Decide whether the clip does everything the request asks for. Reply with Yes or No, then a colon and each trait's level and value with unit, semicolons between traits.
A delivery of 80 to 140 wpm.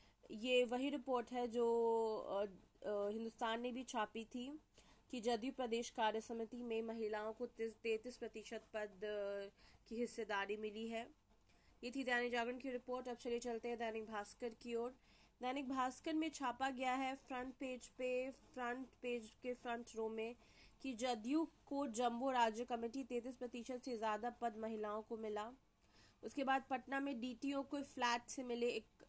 No: average, 160 wpm